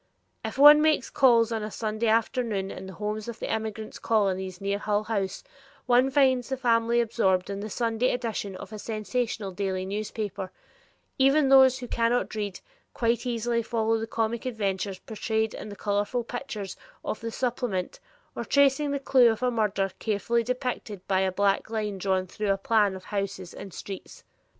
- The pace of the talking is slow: No, average, 180 wpm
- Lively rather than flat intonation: No, average, 3.2 semitones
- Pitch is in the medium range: No, high, 220 Hz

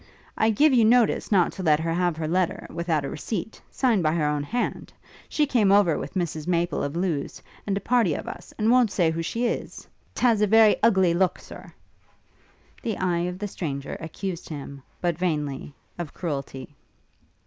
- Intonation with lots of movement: No, average, 5.0 semitones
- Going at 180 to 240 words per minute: Yes, average, 190 wpm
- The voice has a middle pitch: Yes, medium, 175 Hz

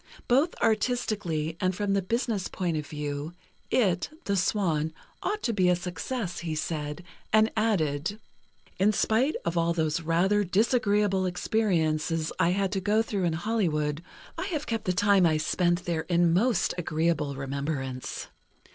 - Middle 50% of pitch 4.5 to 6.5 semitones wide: Yes, average, 4.8 semitones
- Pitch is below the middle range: No, medium, 180 Hz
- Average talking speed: Yes, average, 155 wpm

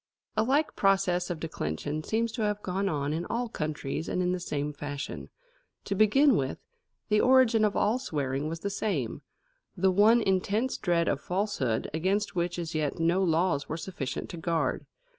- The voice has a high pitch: No, medium, 180 Hz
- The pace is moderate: Yes, average, 180 wpm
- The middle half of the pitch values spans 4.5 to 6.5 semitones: Yes, average, 5.2 semitones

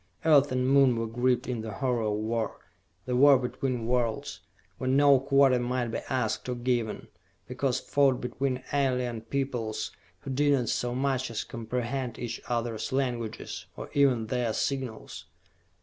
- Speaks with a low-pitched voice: Yes, low, 125 Hz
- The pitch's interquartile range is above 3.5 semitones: No, narrow, 2.4 semitones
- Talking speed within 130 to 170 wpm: Yes, average, 155 wpm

